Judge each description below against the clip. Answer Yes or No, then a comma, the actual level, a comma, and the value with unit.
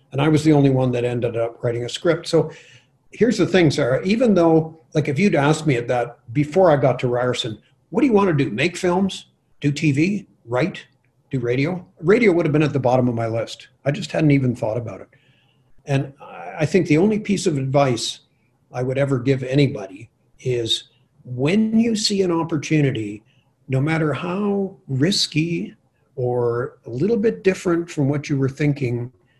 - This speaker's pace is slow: No, average, 190 wpm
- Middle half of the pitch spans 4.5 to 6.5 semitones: Yes, average, 4.8 semitones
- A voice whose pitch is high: No, medium, 140 Hz